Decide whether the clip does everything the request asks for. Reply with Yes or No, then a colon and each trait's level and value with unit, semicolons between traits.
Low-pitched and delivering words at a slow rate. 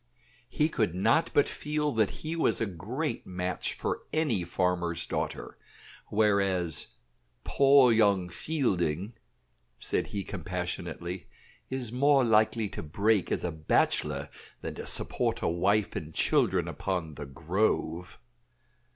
Yes: low, 100 Hz; slow, 125 wpm